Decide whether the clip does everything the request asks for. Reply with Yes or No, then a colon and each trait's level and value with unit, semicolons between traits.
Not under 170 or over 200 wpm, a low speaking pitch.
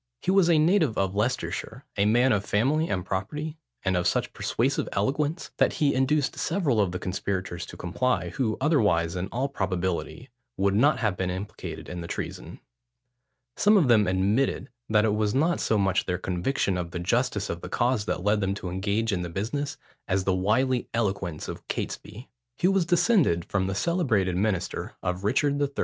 Yes: average, 190 wpm; low, 105 Hz